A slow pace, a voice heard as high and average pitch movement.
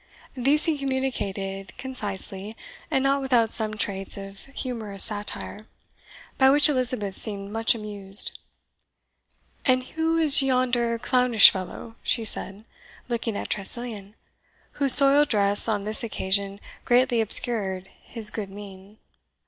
Yes: slow, 125 wpm; high, 225 Hz; average, 4.3 semitones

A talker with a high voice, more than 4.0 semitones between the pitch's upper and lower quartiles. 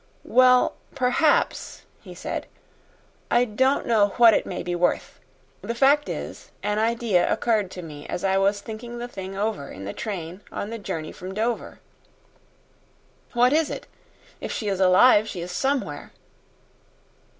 Yes: high, 210 Hz; average, 4.4 semitones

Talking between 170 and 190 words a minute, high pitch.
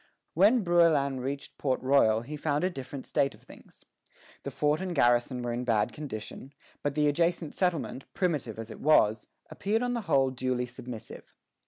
No: average, 175 wpm; medium, 140 Hz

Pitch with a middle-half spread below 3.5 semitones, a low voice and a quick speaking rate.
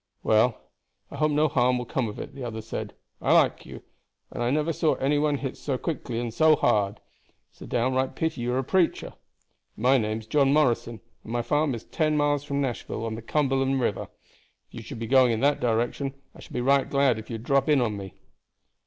No: average, 3.9 semitones; low, 130 Hz; fast, 225 wpm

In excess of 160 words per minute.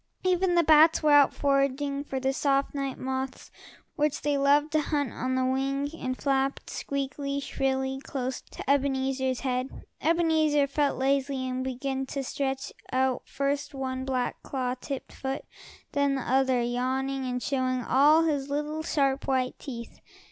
No: average, 155 wpm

